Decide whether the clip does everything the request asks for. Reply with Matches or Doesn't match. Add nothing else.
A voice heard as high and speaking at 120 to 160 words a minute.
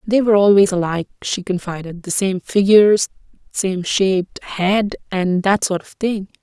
Matches